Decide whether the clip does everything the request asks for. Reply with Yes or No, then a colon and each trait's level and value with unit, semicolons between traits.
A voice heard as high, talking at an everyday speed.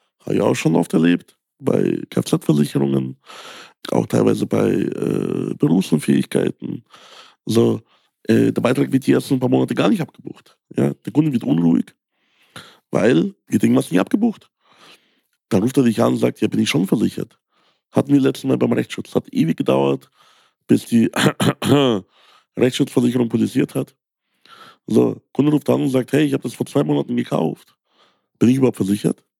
No: low, 115 Hz; average, 175 wpm